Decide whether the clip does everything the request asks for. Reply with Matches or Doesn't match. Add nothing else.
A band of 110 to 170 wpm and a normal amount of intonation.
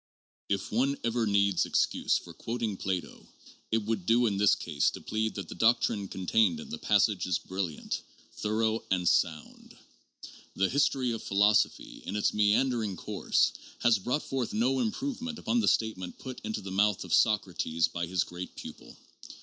Matches